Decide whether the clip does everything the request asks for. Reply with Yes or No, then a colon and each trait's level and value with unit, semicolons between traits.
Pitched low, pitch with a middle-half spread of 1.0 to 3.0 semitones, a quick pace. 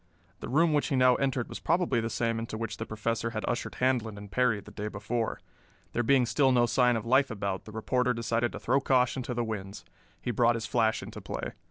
Yes: low, 120 Hz; narrow, 2.4 semitones; fast, 230 wpm